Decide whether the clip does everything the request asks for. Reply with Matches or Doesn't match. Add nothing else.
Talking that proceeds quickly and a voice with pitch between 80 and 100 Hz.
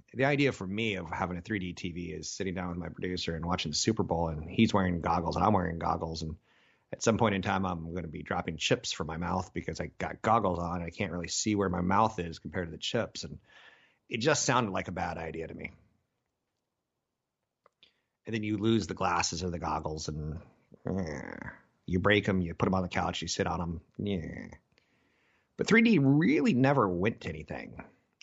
Matches